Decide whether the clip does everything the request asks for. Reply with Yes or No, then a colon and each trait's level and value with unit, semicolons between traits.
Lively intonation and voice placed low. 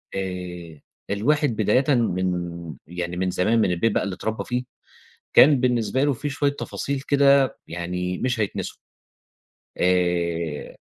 Yes: wide, 6.3 semitones; very low, 95 Hz